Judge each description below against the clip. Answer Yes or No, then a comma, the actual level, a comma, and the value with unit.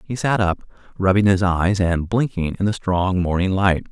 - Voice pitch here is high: No, very low, 95 Hz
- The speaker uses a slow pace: No, average, 200 wpm